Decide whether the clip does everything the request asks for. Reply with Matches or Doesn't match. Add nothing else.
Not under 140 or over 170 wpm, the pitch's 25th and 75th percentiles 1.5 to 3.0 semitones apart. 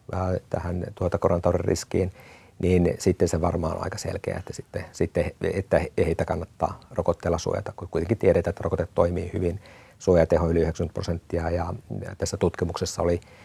Matches